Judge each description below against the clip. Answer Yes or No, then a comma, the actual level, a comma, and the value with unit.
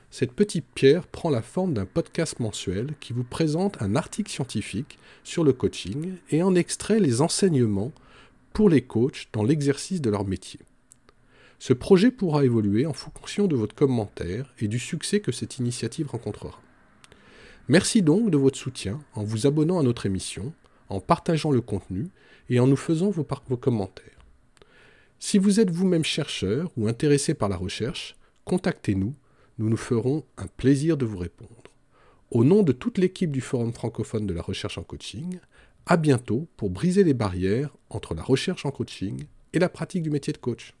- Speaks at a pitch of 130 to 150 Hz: Yes, low, 135 Hz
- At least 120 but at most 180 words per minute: Yes, average, 175 wpm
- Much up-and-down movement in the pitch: Yes, wide, 6.9 semitones